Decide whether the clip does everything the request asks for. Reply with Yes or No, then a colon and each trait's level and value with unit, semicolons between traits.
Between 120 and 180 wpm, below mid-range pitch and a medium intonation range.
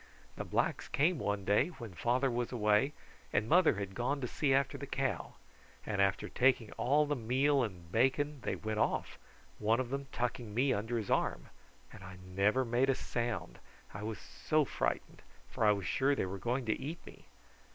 No: average, 195 wpm; low, 120 Hz; average, 4.5 semitones